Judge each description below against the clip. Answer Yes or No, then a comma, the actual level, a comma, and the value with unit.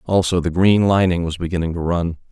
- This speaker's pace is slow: No, fast, 205 wpm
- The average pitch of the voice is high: No, very low, 90 Hz